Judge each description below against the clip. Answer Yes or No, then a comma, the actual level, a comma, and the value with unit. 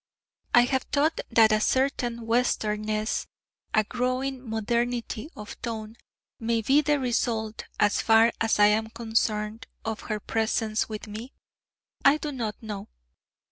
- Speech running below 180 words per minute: Yes, average, 140 wpm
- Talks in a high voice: Yes, high, 225 Hz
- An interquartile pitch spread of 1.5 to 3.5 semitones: Yes, narrow, 2.5 semitones